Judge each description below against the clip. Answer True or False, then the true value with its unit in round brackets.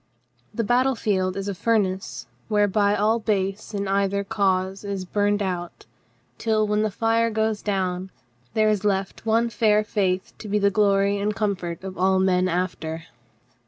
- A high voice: True (200 Hz)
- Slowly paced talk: False (160 wpm)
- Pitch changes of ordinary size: False (2.1 semitones)